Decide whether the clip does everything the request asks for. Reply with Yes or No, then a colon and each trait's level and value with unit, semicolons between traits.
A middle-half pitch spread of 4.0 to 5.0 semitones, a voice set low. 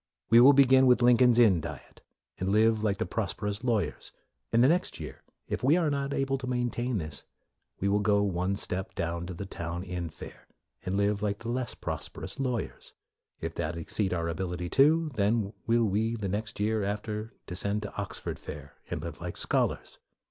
Yes: average, 4.4 semitones; low, 105 Hz